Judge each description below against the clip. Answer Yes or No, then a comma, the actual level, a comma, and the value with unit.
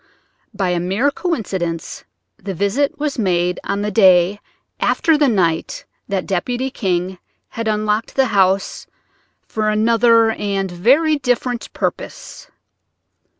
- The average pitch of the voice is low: No, high, 210 Hz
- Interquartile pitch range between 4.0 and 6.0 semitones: Yes, average, 4.6 semitones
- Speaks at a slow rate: Yes, slow, 120 wpm